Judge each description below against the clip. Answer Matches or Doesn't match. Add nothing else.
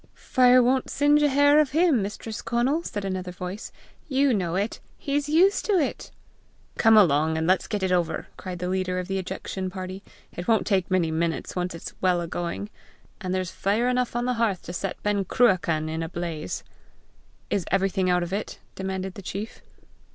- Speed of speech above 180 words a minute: Matches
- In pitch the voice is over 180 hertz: Matches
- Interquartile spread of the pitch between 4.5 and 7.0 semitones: Matches